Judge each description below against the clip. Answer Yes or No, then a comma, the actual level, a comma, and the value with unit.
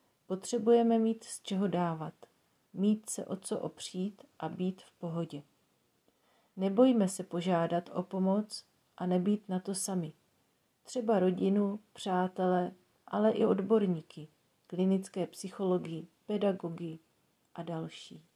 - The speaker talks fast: No, slow, 115 wpm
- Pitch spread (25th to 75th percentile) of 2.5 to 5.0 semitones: Yes, average, 3.2 semitones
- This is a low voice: No, high, 190 Hz